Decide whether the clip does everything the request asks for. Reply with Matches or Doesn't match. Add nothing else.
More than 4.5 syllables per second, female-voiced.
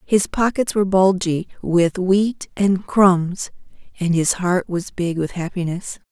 Doesn't match